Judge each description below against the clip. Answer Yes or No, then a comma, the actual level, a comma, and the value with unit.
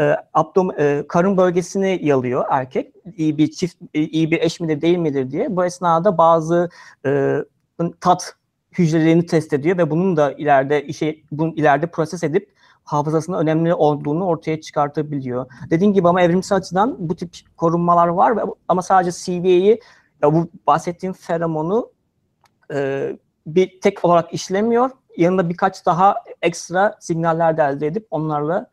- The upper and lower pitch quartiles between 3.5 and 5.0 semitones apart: No, average, 3.0 semitones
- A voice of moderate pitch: Yes, medium, 170 Hz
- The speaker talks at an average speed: No, fast, 145 wpm